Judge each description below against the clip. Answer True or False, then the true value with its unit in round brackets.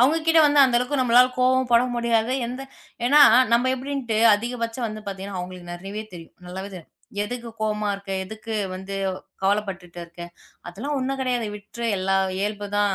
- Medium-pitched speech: False (220 Hz)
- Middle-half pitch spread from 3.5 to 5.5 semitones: True (4.4 semitones)